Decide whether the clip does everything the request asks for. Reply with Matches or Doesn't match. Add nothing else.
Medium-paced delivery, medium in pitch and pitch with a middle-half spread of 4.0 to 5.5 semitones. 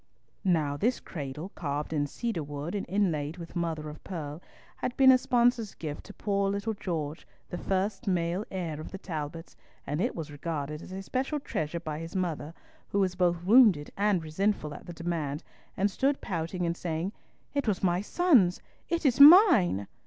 Matches